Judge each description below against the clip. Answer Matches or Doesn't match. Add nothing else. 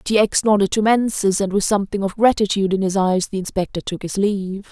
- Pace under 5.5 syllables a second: Doesn't match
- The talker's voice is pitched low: Doesn't match